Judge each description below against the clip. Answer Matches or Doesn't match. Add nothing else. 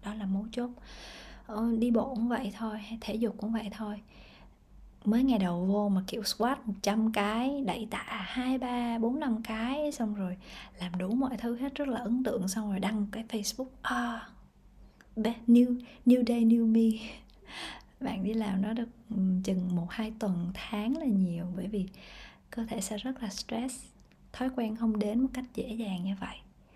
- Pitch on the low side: Doesn't match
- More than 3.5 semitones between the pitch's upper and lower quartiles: Doesn't match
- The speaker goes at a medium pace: Matches